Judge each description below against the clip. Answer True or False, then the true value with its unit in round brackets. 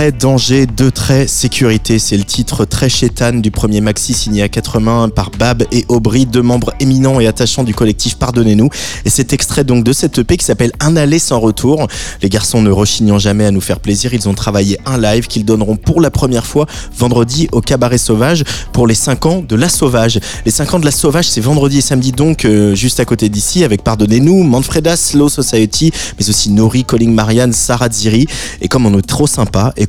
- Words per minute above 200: True (215 wpm)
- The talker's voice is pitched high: False (120 Hz)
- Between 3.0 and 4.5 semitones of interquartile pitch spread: True (3.7 semitones)